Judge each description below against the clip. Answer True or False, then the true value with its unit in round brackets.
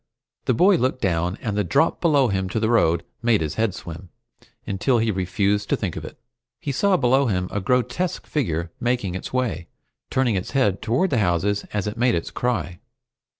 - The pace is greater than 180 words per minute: True (195 wpm)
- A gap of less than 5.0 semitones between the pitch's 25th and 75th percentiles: False (5.3 semitones)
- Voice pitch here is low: True (105 Hz)